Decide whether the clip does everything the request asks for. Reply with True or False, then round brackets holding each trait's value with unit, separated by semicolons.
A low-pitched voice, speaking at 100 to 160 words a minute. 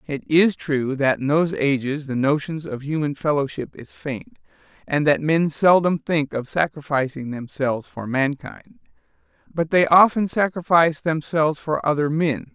False (150 Hz; 155 wpm)